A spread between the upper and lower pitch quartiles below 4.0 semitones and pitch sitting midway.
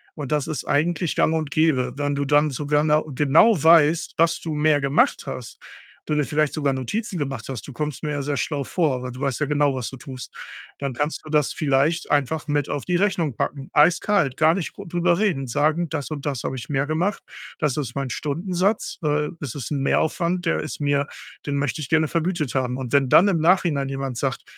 Yes: average, 2.8 semitones; medium, 150 Hz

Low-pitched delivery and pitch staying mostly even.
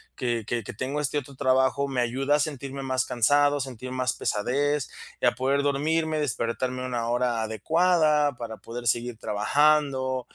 No: low, 130 Hz; average, 3.0 semitones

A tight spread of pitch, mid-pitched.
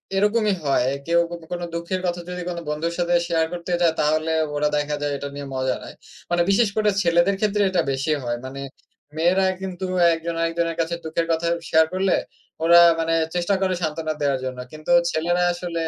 Yes: narrow, 2.2 semitones; medium, 170 Hz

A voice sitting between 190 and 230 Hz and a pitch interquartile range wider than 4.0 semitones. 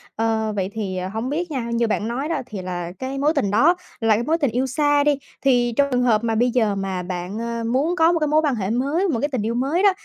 No: high, 245 Hz; average, 4.9 semitones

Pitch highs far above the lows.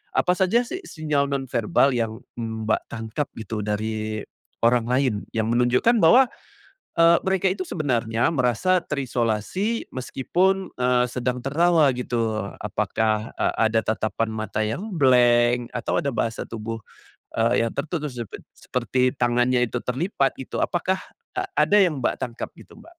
Yes: wide, 5.7 semitones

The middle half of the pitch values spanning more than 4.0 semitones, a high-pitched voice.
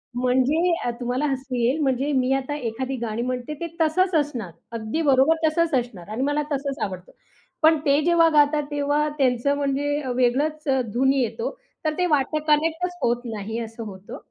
No: average, 3.7 semitones; very high, 270 Hz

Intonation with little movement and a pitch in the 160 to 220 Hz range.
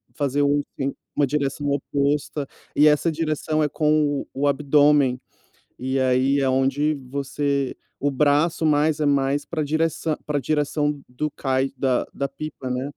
No: narrow, 1.7 semitones; medium, 145 Hz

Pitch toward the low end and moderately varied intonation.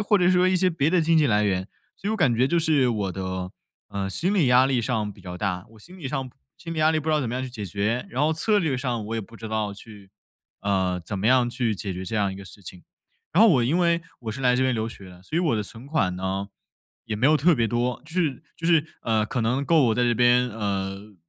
No: low, 120 Hz; wide, 7.0 semitones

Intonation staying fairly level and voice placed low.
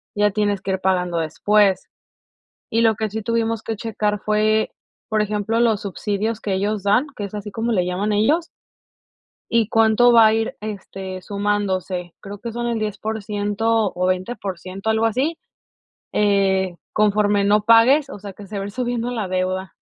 No: narrow, 2.3 semitones; high, 210 Hz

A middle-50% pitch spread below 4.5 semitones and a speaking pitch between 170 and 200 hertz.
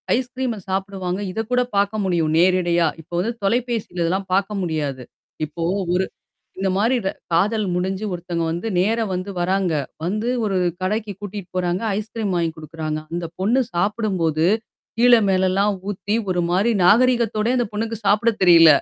Yes: average, 3.8 semitones; high, 195 Hz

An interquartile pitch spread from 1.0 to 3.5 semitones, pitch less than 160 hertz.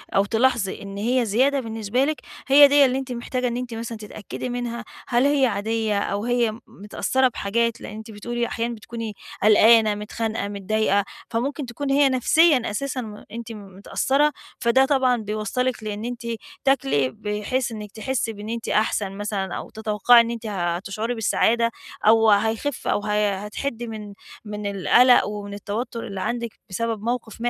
No: average, 2.8 semitones; high, 225 Hz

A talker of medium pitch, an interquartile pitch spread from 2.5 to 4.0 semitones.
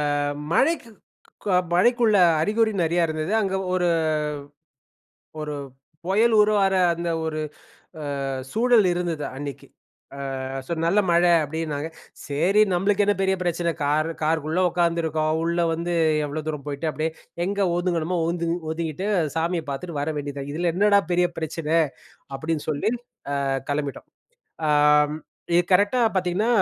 Yes: medium, 170 Hz; average, 3.7 semitones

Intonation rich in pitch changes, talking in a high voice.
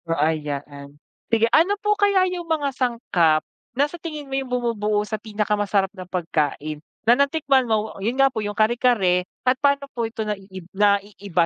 Yes: wide, 6.2 semitones; high, 215 Hz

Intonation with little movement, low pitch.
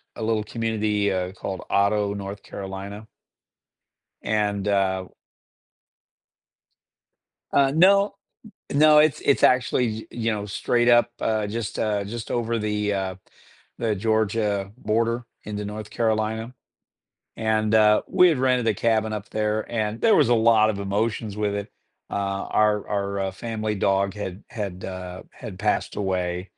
Yes: narrow, 2.2 semitones; low, 105 Hz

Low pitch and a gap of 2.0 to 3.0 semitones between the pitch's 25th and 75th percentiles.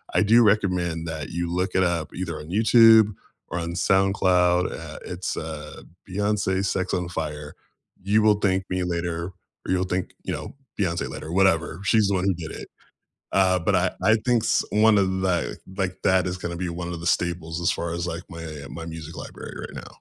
Yes: very low, 90 Hz; narrow, 2.4 semitones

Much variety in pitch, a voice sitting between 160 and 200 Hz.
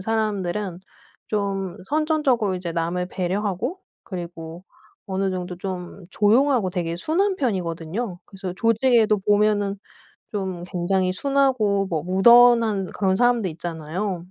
No: average, 3.9 semitones; high, 195 Hz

